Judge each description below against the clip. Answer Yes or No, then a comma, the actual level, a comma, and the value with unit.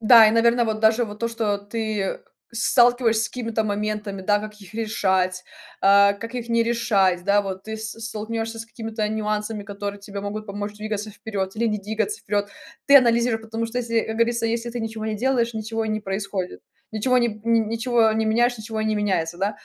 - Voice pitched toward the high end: Yes, high, 220 Hz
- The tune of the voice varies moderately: No, narrow, 1.9 semitones